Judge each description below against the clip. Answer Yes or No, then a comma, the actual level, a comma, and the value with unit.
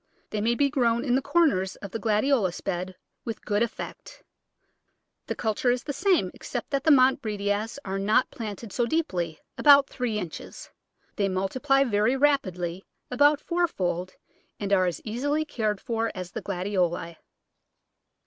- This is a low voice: No, high, 220 Hz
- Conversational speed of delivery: Yes, average, 160 wpm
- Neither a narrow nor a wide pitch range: No, wide, 5.9 semitones